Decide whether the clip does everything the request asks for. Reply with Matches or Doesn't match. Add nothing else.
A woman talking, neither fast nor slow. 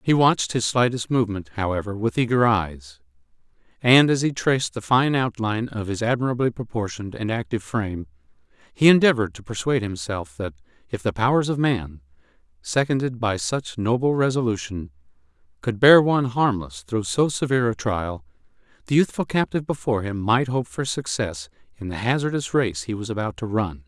Doesn't match